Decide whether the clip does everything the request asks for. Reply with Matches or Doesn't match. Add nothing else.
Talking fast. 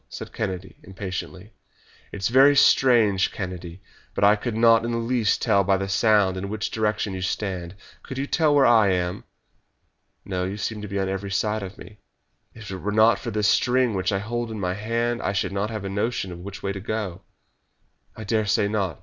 Matches